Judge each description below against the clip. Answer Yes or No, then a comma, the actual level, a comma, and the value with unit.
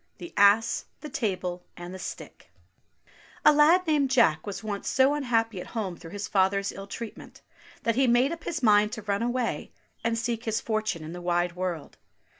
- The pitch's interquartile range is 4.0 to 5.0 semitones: Yes, average, 4.7 semitones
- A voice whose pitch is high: Yes, high, 215 Hz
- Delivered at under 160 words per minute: No, average, 190 wpm